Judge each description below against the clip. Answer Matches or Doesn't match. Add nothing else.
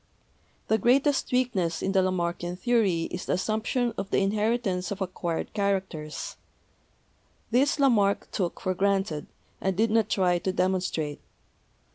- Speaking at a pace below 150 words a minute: Matches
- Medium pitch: Doesn't match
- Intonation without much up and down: Doesn't match